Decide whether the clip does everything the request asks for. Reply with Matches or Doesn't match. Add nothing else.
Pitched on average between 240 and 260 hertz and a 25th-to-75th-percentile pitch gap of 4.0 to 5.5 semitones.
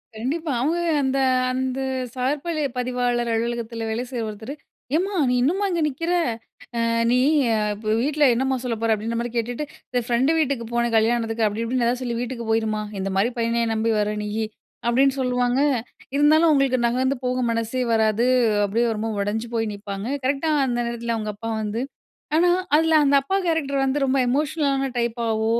Doesn't match